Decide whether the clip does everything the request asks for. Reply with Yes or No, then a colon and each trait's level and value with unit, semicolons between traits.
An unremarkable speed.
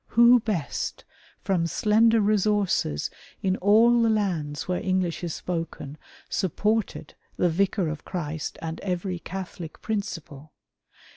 No: slow, 120 wpm